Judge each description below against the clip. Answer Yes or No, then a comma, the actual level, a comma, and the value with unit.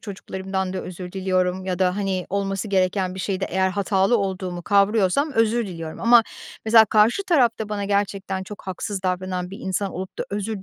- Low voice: No, high, 195 Hz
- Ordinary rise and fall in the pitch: No, narrow, 1.9 semitones